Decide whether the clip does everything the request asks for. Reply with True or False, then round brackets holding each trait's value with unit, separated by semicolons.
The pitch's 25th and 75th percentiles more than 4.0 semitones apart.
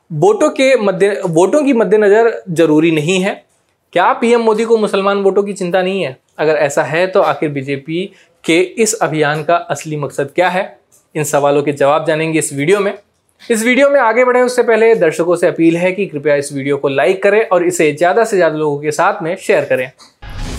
True (5.1 semitones)